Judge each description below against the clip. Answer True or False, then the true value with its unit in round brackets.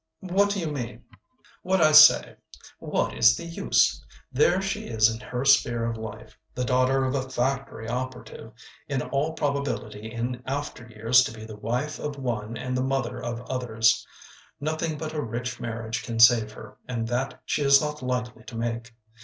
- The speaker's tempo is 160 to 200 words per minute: True (180 wpm)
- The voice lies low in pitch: True (125 Hz)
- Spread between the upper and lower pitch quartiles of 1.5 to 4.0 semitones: True (3.5 semitones)